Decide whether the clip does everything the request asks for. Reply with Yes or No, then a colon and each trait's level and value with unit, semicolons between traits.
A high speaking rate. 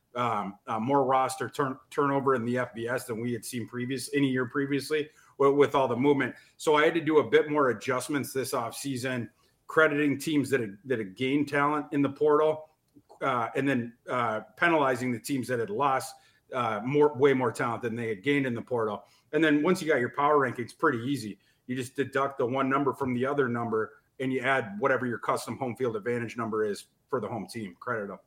Yes: fast, 220 wpm